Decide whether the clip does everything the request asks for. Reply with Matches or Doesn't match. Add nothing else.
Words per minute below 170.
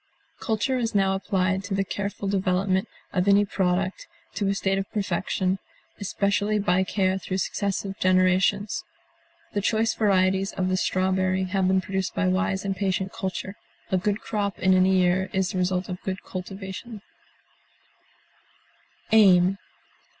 Matches